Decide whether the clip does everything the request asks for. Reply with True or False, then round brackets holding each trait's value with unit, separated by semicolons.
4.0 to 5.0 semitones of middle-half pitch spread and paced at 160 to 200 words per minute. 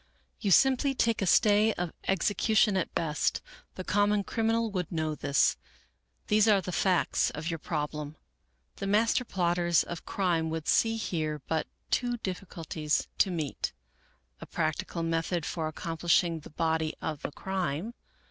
False (4.4 semitones; 150 wpm)